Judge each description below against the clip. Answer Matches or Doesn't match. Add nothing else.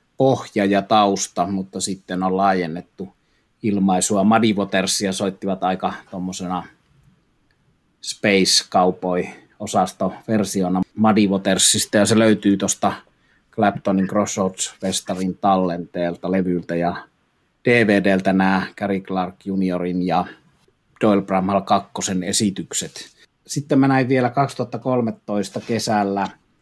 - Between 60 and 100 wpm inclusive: Matches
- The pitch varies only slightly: Matches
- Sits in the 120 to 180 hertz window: Doesn't match